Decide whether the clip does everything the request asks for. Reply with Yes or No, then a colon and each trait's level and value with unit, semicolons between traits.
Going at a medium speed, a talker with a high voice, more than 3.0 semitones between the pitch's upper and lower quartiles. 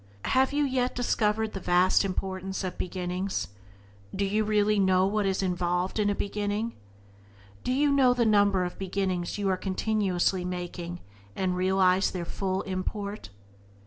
No: average, 150 wpm; high, 195 Hz; narrow, 2.4 semitones